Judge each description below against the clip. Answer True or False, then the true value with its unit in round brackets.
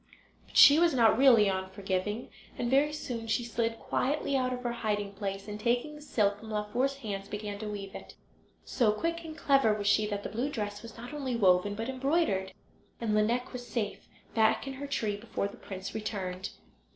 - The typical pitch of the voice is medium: False (220 Hz)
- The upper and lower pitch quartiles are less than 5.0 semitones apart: True (3.9 semitones)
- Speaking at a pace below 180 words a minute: False (200 wpm)